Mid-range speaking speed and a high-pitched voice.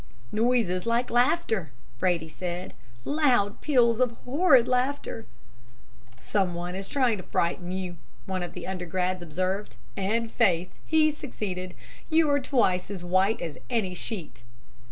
No: slow, 130 wpm; high, 200 Hz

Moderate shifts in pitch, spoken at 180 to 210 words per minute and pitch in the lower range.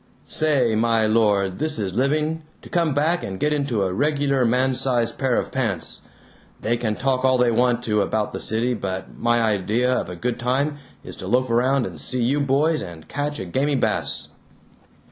Yes: average, 4.2 semitones; average, 195 wpm; low, 125 Hz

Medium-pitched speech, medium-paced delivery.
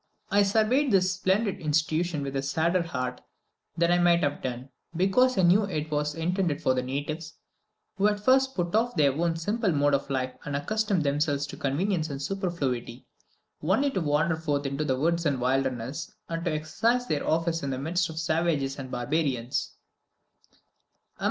Yes: medium, 160 Hz; average, 175 wpm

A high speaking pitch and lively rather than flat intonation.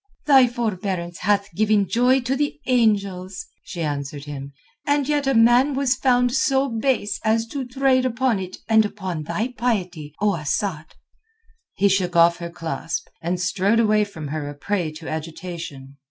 Yes: high, 205 Hz; wide, 6.4 semitones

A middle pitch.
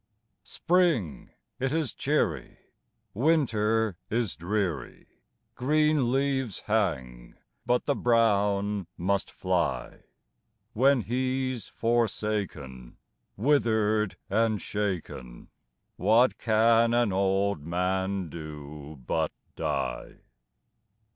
No: low, 105 Hz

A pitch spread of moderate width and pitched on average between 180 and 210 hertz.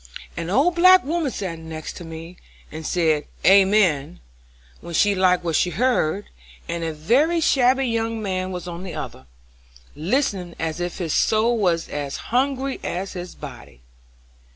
No: wide, 6.2 semitones; medium, 185 Hz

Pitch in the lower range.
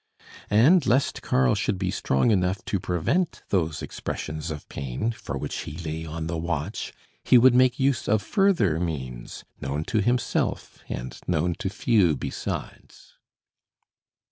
Yes: very low, 90 Hz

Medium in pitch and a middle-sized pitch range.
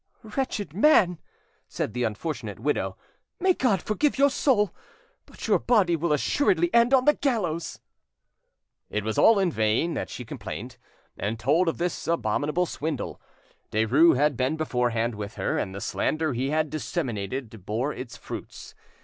No: medium, 155 Hz; wide, 7.8 semitones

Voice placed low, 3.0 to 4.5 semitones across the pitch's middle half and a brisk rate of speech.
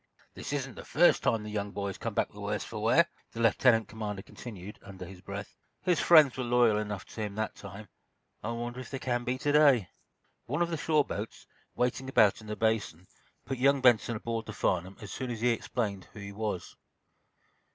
Yes: low, 110 Hz; average, 3.5 semitones; fast, 215 wpm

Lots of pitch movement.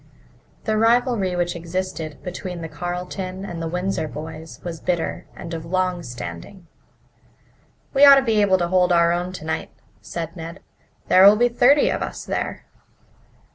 No: narrow, 2.6 semitones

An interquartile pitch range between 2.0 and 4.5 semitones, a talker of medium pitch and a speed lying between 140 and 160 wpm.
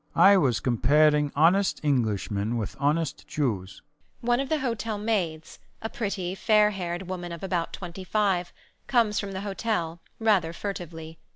No: average, 5.2 semitones; medium, 175 Hz; average, 145 wpm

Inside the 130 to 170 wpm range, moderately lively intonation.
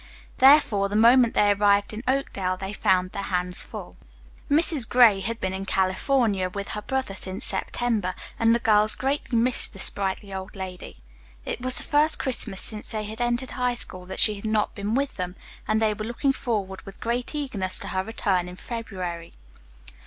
No: average, 190 wpm; average, 4.1 semitones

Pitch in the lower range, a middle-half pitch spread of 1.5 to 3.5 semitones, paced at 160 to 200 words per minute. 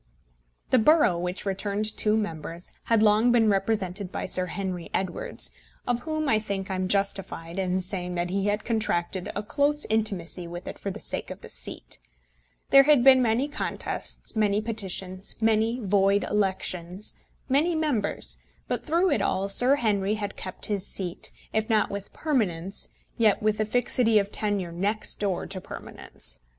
No: high, 205 Hz; average, 3.2 semitones; average, 165 wpm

